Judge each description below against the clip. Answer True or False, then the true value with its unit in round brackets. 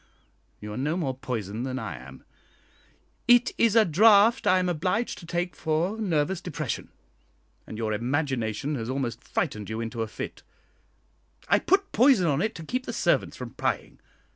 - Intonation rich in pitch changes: True (8.5 semitones)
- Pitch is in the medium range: True (150 Hz)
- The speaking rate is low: False (170 wpm)